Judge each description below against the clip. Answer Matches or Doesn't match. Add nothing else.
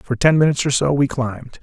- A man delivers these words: Matches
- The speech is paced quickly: Matches